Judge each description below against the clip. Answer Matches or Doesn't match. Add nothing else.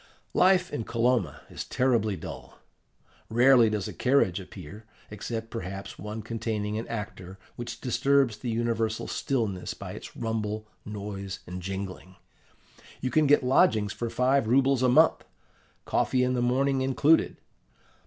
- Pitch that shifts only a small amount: Doesn't match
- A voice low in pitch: Matches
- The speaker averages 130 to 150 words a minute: Matches